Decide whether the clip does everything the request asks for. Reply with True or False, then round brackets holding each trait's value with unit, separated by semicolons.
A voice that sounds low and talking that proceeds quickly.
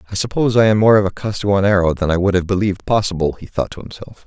True (100 Hz; 255 wpm)